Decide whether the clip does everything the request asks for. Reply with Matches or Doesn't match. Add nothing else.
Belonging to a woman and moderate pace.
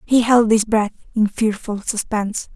Matches